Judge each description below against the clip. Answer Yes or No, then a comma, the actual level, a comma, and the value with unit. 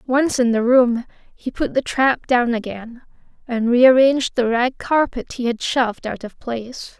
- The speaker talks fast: No, average, 180 wpm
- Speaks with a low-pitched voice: No, high, 245 Hz